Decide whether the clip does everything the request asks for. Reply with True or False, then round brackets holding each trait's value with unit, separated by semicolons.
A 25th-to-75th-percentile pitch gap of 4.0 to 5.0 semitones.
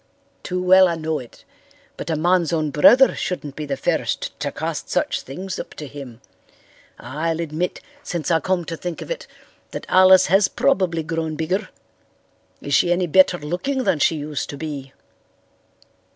False (3.4 semitones)